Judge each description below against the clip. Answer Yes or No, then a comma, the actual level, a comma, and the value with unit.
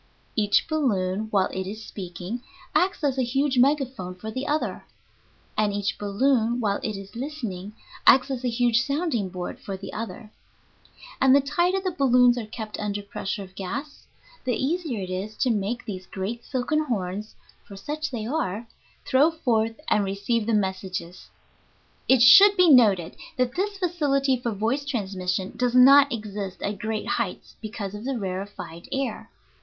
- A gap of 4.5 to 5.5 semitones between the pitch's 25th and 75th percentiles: Yes, average, 5.2 semitones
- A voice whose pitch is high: Yes, high, 230 Hz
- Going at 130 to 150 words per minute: No, average, 165 wpm